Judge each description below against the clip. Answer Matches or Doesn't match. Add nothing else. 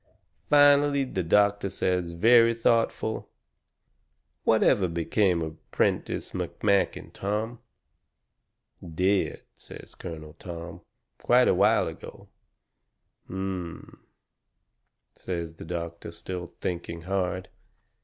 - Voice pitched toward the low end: Matches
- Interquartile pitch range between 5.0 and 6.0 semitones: Doesn't match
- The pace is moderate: Doesn't match